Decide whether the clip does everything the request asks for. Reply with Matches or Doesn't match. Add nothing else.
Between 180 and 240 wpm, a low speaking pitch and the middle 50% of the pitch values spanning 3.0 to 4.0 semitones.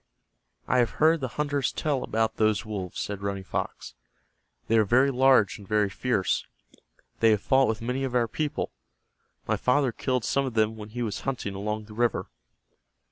Matches